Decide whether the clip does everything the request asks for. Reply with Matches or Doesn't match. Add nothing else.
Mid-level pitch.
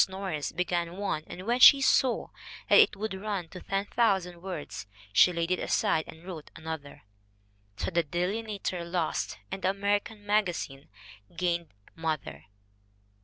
Matches